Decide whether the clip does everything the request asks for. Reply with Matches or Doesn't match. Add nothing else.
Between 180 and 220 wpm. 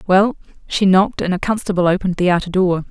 Matches